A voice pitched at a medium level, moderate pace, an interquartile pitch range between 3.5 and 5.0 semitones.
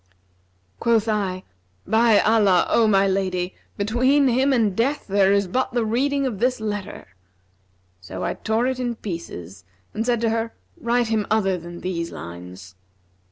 No: high, 215 Hz; average, 160 wpm; average, 4.3 semitones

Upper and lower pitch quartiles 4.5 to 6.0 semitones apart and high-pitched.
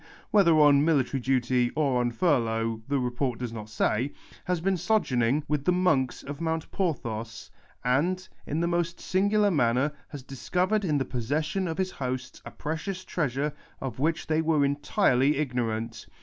No: average, 5.2 semitones; medium, 145 Hz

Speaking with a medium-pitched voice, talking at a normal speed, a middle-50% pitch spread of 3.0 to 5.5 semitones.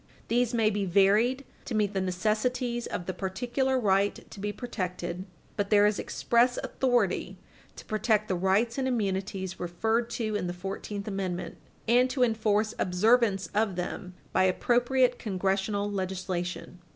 No: high, 205 Hz; average, 150 wpm; average, 3.8 semitones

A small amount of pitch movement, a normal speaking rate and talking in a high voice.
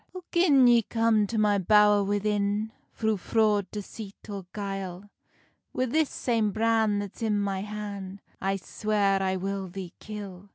Yes: narrow, 1.9 semitones; average, 155 wpm; high, 205 Hz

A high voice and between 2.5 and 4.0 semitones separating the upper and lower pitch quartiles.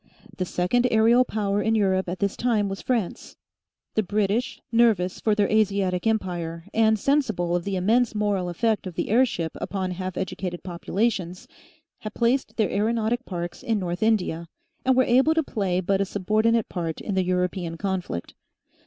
Yes: high, 200 Hz; average, 3.7 semitones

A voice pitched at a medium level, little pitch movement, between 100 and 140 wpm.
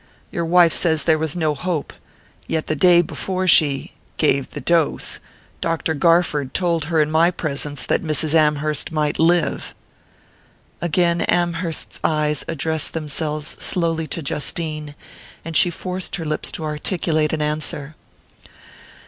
Yes: medium, 160 Hz; narrow, 2.0 semitones; slow, 135 wpm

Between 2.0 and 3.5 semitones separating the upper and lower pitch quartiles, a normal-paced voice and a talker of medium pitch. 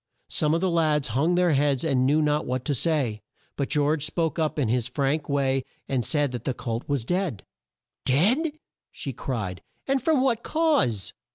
No: average, 4.5 semitones; average, 185 wpm; medium, 145 Hz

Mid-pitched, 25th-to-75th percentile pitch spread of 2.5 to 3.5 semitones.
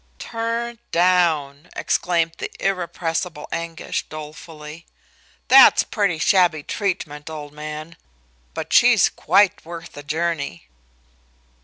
Yes: medium, 165 Hz; average, 2.9 semitones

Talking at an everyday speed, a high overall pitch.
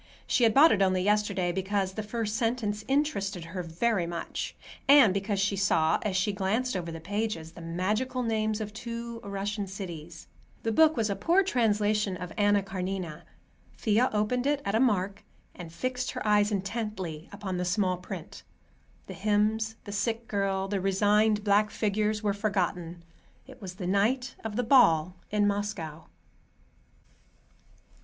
Yes: average, 160 wpm; high, 205 Hz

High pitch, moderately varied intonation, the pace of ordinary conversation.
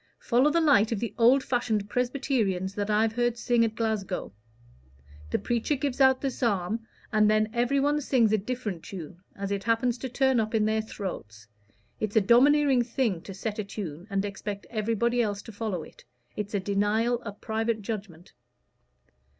Yes: high, 220 Hz; average, 3.2 semitones; average, 175 wpm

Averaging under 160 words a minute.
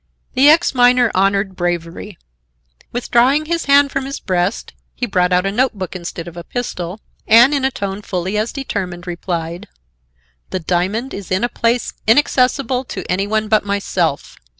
No: average, 170 wpm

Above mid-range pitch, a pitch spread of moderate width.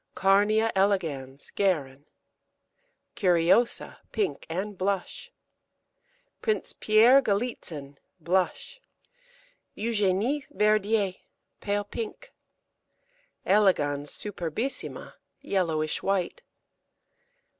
Yes: high, 200 Hz; average, 4.3 semitones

